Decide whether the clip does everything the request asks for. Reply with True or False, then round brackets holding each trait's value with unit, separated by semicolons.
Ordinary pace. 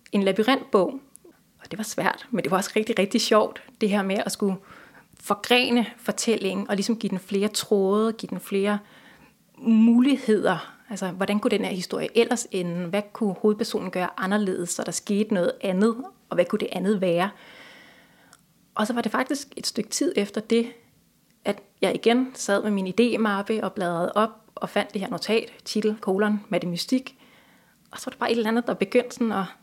True (190 wpm)